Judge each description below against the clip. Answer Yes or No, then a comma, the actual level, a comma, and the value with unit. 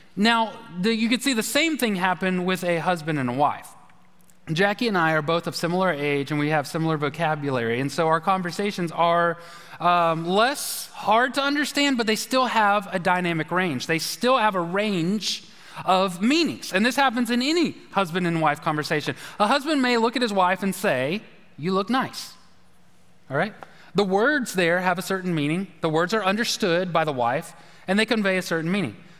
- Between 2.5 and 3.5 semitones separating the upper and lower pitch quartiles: No, average, 4.8 semitones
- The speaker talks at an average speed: Yes, average, 195 wpm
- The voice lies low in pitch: No, medium, 185 Hz